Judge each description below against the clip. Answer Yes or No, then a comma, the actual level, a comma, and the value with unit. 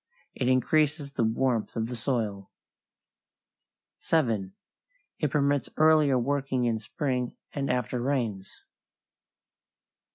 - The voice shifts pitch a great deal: No, average, 3.7 semitones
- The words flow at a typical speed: No, slow, 100 wpm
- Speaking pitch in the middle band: No, low, 130 Hz